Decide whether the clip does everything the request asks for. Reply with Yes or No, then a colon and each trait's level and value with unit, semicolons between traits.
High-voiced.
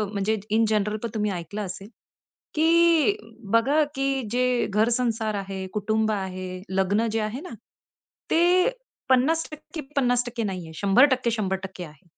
Yes: high, 220 Hz